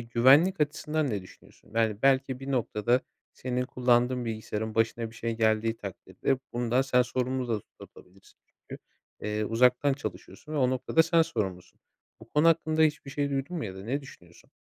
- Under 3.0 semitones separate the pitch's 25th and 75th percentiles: No, average, 3.8 semitones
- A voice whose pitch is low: Yes, low, 125 Hz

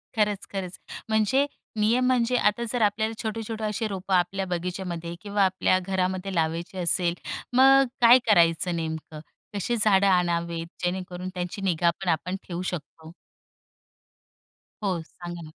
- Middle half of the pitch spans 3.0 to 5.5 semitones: Yes, average, 3.5 semitones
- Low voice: No, medium, 185 Hz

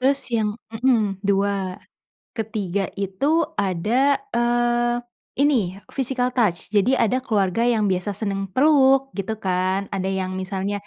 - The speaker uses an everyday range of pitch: Yes, average, 4.3 semitones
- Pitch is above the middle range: Yes, high, 210 Hz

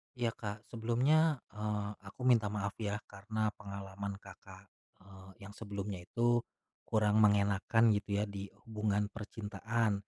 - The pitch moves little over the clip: Yes, narrow, 1.9 semitones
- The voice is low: Yes, low, 105 Hz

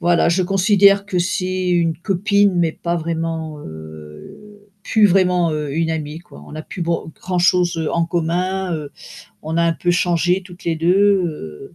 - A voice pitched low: No, medium, 175 Hz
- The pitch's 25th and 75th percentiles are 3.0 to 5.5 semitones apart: No, narrow, 2.4 semitones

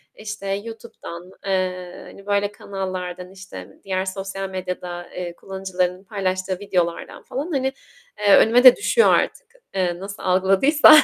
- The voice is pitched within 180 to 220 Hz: Yes, high, 190 Hz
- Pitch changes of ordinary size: No, narrow, 2.0 semitones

